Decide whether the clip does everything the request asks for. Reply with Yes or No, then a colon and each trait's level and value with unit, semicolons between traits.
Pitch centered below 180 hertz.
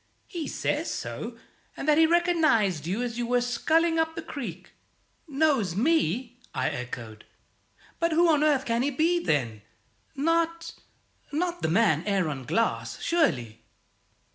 No: very high, 265 Hz